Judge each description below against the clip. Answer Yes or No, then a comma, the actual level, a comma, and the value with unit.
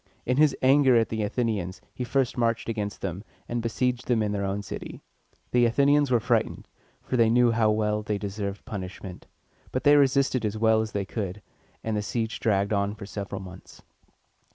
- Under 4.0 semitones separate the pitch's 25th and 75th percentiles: Yes, average, 3.3 semitones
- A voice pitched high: No, low, 110 Hz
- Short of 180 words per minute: No, average, 190 wpm